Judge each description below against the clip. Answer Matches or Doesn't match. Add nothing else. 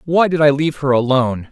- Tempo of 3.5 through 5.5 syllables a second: Doesn't match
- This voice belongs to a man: Matches